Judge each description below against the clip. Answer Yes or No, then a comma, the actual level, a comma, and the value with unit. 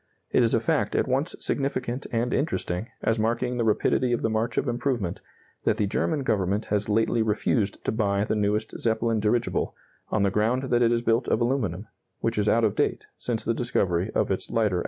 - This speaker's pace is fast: Yes, fast, 210 wpm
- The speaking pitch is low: Yes, low, 115 Hz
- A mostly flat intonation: Yes, narrow, 2.3 semitones